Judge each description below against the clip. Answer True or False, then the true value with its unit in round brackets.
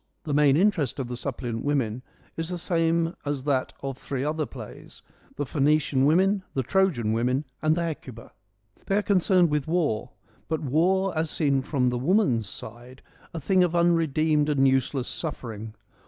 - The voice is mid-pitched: True (145 Hz)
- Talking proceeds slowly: False (170 wpm)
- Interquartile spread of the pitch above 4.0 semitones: True (4.4 semitones)